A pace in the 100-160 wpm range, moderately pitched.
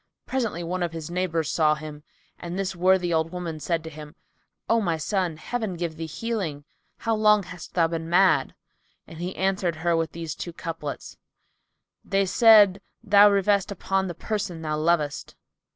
No: average, 170 wpm; medium, 175 Hz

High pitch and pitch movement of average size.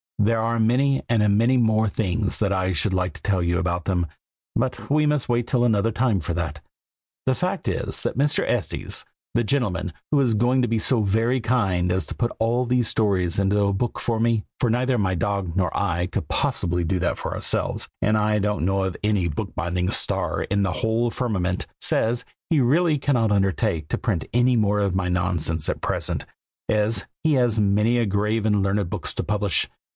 No: low, 105 Hz; average, 4.0 semitones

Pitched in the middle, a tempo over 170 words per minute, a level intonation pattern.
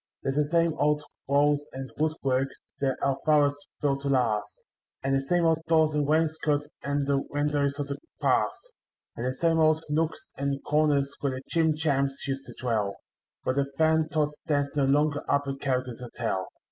Yes: medium, 145 Hz; average, 180 wpm; narrow, 2.2 semitones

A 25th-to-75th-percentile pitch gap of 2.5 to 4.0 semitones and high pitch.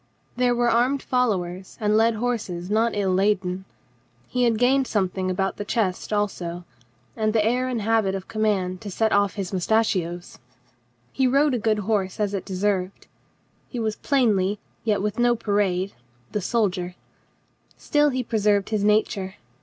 Yes: average, 3.3 semitones; high, 210 Hz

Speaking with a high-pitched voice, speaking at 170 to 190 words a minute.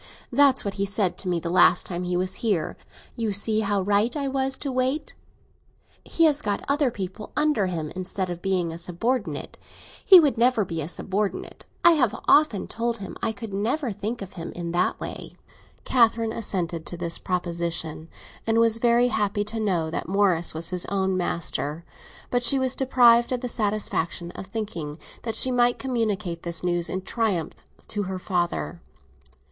Yes: high, 205 Hz; average, 180 wpm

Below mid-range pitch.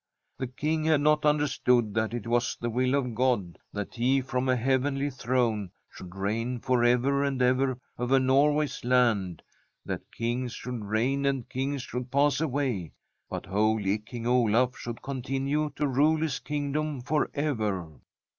Yes: low, 125 Hz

